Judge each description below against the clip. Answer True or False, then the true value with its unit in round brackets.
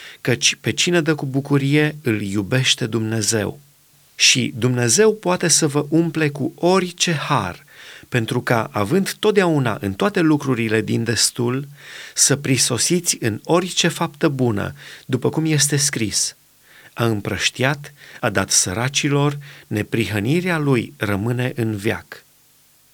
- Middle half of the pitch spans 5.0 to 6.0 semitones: True (5.4 semitones)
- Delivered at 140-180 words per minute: False (125 wpm)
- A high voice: False (135 Hz)